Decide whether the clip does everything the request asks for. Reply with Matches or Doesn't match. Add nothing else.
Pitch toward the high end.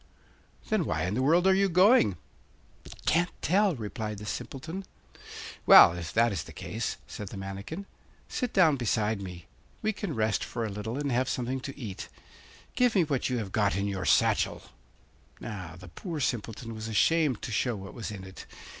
Doesn't match